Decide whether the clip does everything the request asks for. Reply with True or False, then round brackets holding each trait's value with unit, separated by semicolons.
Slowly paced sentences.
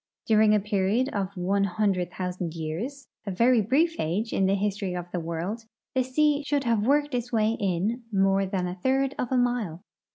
False (200 wpm)